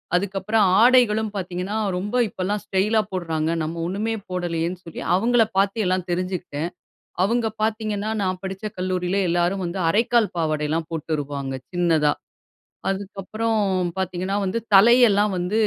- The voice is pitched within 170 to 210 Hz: Yes, high, 190 Hz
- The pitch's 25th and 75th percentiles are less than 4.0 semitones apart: Yes, average, 3.4 semitones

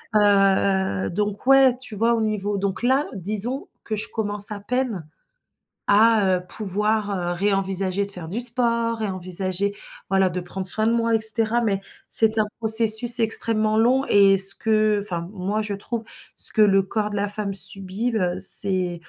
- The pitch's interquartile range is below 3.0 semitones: Yes, narrow, 2.6 semitones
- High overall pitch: Yes, high, 210 Hz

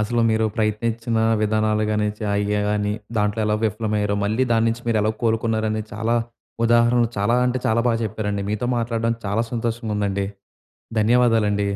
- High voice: No, low, 110 Hz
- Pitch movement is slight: Yes, narrow, 1.7 semitones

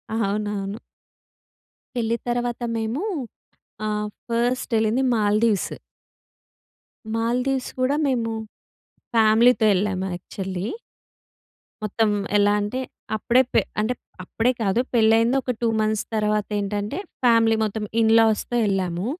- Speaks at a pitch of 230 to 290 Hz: No, high, 220 Hz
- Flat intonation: Yes, narrow, 2.3 semitones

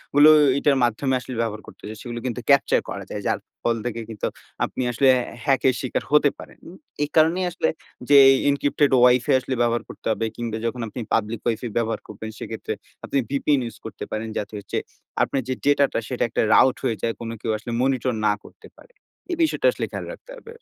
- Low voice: Yes, low, 125 Hz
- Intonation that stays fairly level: No, average, 3.8 semitones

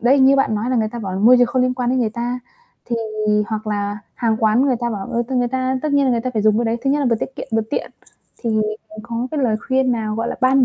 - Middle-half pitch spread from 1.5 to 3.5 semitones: Yes, average, 2.8 semitones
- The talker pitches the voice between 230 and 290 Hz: Yes, high, 240 Hz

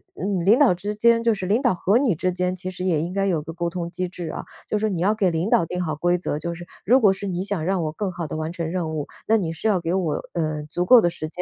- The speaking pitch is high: No, medium, 180 Hz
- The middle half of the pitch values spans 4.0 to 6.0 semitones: No, average, 3.3 semitones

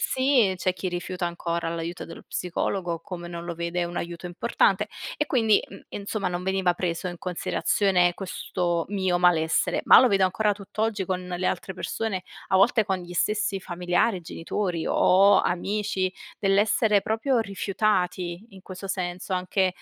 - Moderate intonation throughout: No, narrow, 2.3 semitones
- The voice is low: No, medium, 185 Hz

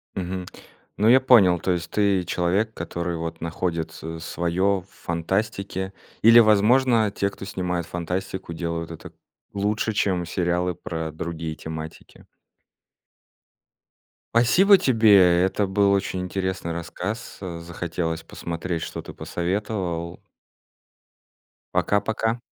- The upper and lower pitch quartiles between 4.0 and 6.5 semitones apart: No, average, 3.2 semitones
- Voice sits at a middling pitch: No, very low, 90 Hz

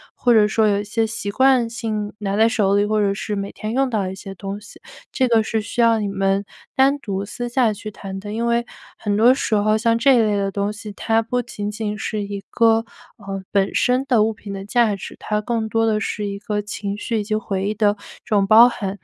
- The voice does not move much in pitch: Yes, narrow, 2.1 semitones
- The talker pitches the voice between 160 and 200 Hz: No, high, 215 Hz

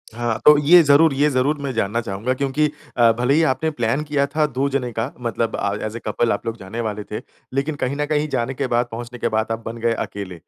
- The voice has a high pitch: No, low, 125 Hz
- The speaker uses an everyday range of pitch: Yes, average, 3.9 semitones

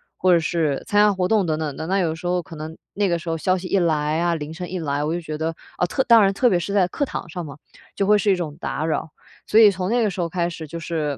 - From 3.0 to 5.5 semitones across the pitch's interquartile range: Yes, average, 3.3 semitones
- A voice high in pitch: No, medium, 175 Hz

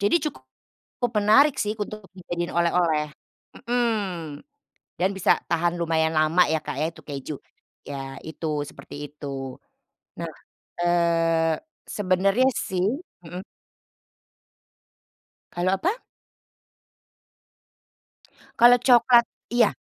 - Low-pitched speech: No, medium, 175 Hz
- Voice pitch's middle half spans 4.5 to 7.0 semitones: Yes, average, 4.8 semitones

